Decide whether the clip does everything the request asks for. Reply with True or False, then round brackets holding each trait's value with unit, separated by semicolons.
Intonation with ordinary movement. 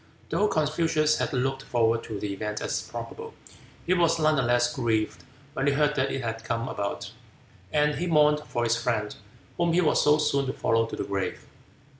True (5.0 semitones)